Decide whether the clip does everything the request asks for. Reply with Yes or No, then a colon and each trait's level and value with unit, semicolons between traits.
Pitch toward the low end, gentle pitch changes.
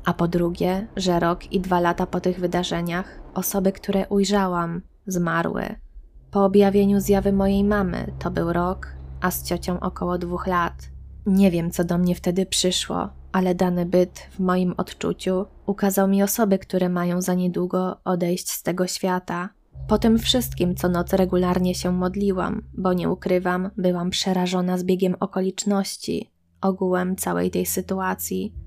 No: medium, 180 Hz; narrow, 1.5 semitones